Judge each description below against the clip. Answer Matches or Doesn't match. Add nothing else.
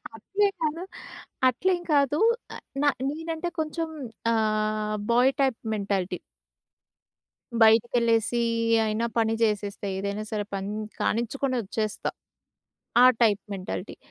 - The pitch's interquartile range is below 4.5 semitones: Doesn't match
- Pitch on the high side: Matches